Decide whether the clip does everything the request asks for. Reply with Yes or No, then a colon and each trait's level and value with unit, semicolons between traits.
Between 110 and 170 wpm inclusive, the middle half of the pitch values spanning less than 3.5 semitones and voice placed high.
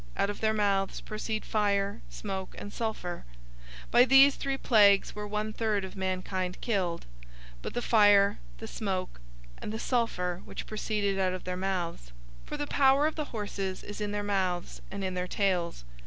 No: average, 185 wpm; narrow, 2.6 semitones; high, 205 Hz